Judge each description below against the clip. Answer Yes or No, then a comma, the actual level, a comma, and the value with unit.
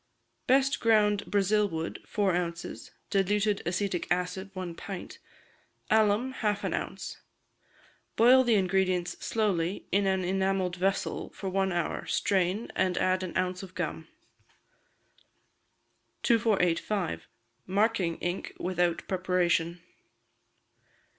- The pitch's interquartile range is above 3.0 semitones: No, narrow, 2.5 semitones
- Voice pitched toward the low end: No, high, 190 Hz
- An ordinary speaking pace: No, slow, 110 wpm